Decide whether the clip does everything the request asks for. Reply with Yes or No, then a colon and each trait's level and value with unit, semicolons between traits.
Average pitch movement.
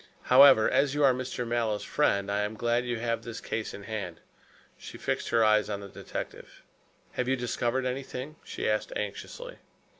Yes: average, 3.3 semitones